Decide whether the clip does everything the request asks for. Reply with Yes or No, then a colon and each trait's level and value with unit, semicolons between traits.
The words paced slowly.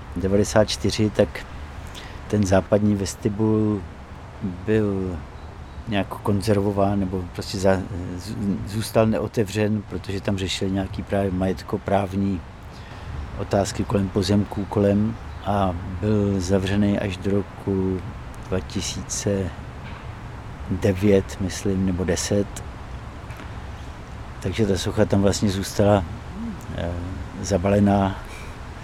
Yes: slow, 85 wpm